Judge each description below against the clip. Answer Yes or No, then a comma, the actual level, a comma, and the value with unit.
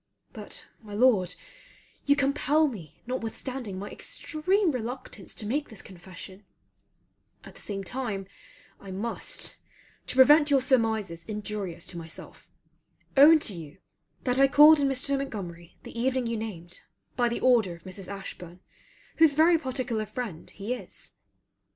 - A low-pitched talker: No, high, 230 Hz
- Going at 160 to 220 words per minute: No, average, 145 wpm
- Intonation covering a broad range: Yes, wide, 5.8 semitones